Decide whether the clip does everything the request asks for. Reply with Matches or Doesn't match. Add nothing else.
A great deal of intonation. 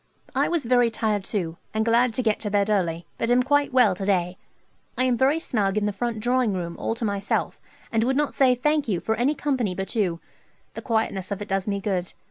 Doesn't match